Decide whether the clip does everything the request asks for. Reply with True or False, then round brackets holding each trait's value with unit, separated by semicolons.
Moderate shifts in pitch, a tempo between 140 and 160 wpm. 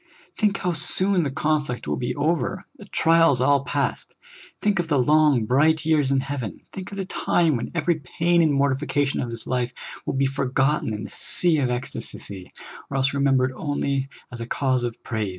False (3.9 semitones; 195 wpm)